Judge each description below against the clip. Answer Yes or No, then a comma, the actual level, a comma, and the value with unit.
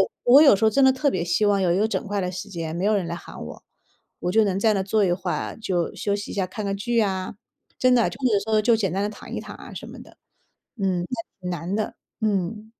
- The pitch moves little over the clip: No, average, 3.1 semitones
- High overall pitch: Yes, high, 200 Hz